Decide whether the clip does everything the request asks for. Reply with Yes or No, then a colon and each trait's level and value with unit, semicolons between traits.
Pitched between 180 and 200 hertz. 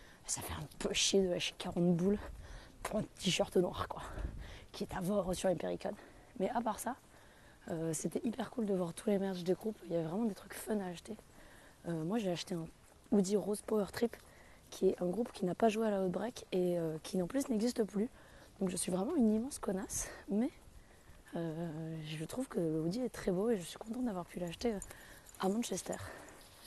Yes: high, 190 Hz